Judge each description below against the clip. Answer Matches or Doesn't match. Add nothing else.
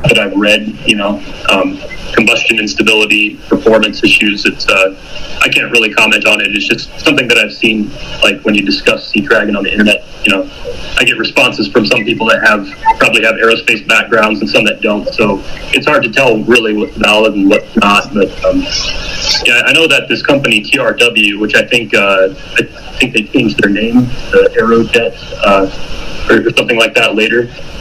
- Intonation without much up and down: Matches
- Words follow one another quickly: Doesn't match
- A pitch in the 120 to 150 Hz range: Doesn't match